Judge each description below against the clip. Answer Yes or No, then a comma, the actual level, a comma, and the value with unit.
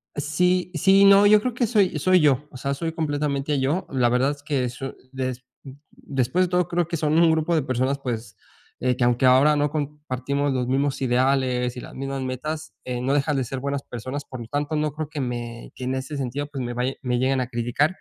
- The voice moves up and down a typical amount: Yes, average, 3.1 semitones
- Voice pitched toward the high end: No, medium, 140 Hz